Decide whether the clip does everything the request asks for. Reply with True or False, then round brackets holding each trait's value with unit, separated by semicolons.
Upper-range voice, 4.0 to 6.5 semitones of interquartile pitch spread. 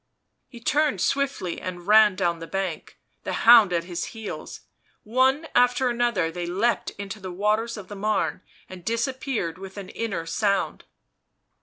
True (205 Hz; 4.6 semitones)